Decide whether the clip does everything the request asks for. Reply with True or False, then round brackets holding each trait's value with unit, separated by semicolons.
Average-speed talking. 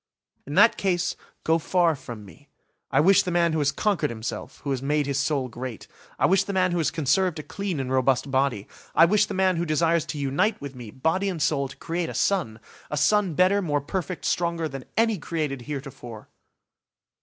False (210 wpm)